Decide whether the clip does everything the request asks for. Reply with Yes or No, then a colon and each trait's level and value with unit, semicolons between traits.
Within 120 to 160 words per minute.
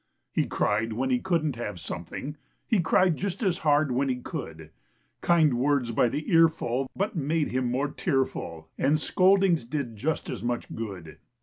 No: average, 170 wpm